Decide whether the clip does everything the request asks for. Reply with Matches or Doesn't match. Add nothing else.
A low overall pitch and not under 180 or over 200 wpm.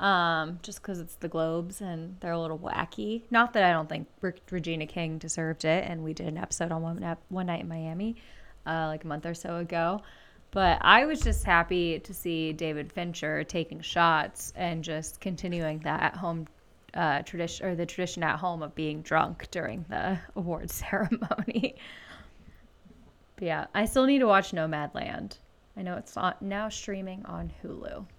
Doesn't match